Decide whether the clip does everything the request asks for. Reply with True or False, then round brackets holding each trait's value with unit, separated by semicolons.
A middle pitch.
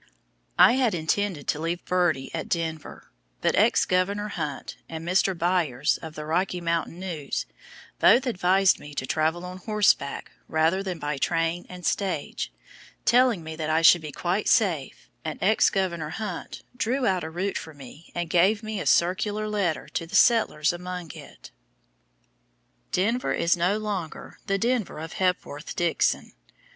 True (175 Hz)